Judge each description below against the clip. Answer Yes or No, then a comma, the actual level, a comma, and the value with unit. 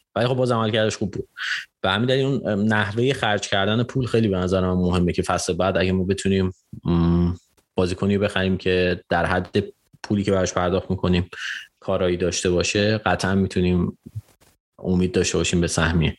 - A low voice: Yes, very low, 95 Hz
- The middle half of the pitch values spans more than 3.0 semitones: No, average, 2.7 semitones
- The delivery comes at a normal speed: No, fast, 175 wpm